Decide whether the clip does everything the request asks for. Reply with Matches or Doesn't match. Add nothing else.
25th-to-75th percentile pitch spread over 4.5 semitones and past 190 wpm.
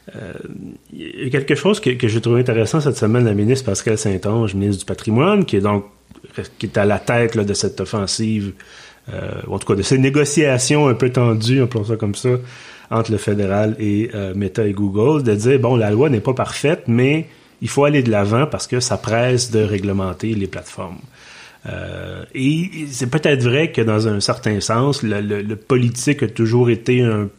Doesn't match